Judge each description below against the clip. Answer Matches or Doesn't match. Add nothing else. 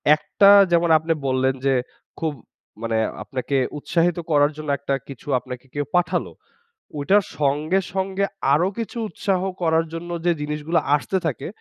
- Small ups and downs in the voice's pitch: Doesn't match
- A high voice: Doesn't match